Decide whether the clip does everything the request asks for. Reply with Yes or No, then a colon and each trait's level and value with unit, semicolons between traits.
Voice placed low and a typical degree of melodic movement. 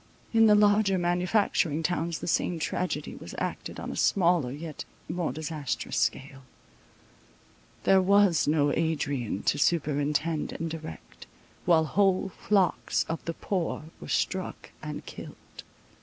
No: medium, 165 Hz; average, 3.6 semitones